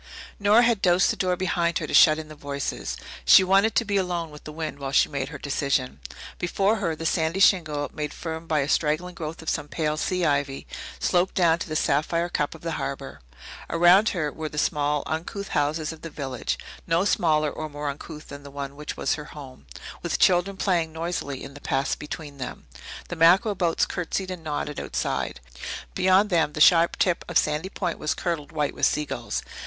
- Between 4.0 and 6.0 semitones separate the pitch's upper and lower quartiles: No, average, 3.2 semitones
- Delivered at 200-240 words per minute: Yes, fast, 205 wpm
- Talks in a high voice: No, medium, 160 Hz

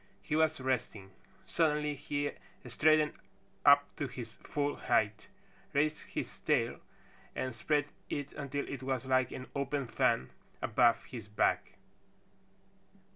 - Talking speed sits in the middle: No, slow, 125 wpm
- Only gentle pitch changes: No, average, 3.1 semitones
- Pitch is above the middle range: No, medium, 140 Hz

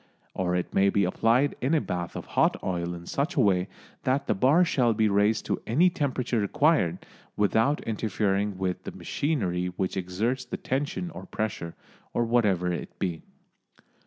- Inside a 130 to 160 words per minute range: No, average, 170 wpm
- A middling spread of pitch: No, wide, 6.3 semitones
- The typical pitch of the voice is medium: No, low, 105 Hz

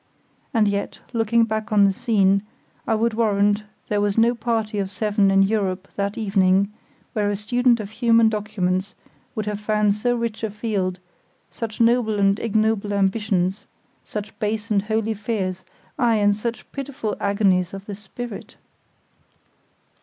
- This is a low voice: No, high, 210 Hz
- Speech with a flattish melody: Yes, narrow, 2.0 semitones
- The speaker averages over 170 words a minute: No, average, 155 wpm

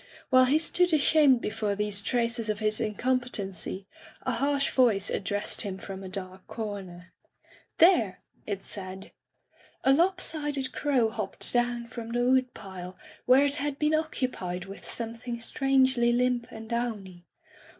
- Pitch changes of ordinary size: Yes, average, 4.6 semitones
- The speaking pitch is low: No, high, 235 Hz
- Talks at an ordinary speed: Yes, average, 145 wpm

